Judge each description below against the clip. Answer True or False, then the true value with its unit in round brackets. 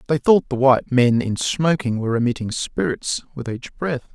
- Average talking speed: True (190 wpm)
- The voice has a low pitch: True (130 Hz)